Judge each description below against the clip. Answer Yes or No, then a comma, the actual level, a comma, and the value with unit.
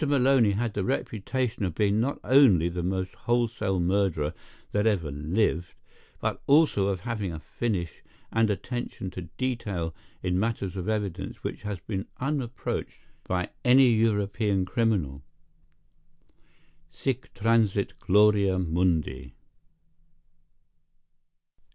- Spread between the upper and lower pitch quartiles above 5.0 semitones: No, average, 4.1 semitones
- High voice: No, low, 100 Hz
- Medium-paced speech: No, slow, 115 wpm